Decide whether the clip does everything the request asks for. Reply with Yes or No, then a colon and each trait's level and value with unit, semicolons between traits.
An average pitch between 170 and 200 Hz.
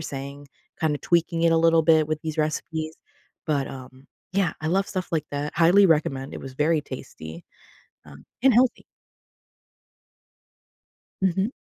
No: medium, 155 Hz